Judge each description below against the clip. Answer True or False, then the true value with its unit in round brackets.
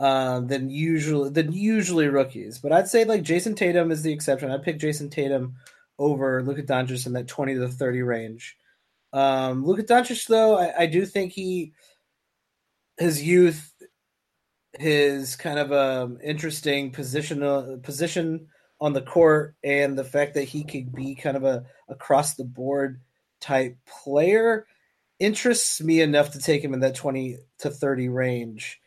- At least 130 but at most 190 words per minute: True (165 wpm)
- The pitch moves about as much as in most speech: True (3.4 semitones)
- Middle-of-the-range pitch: True (145 Hz)